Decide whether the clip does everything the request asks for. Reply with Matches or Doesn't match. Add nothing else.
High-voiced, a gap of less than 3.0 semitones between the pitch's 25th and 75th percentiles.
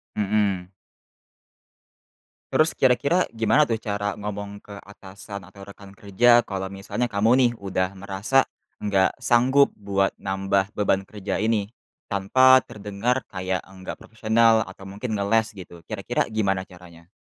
Doesn't match